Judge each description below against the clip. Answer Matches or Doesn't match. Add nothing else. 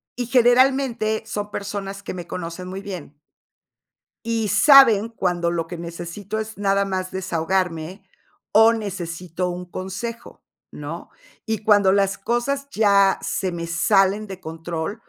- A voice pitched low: Doesn't match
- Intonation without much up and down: Doesn't match